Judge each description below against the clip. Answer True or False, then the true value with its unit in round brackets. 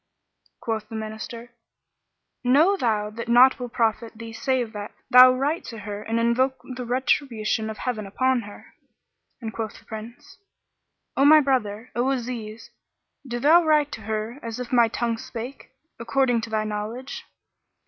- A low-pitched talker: False (235 Hz)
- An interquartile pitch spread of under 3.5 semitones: True (2.9 semitones)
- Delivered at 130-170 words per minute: True (160 wpm)